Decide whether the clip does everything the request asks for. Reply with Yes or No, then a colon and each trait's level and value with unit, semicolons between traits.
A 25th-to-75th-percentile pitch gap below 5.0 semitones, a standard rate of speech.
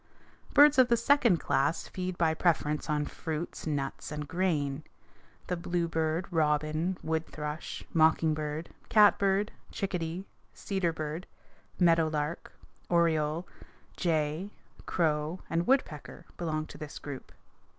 No: average, 2.8 semitones; slow, 120 wpm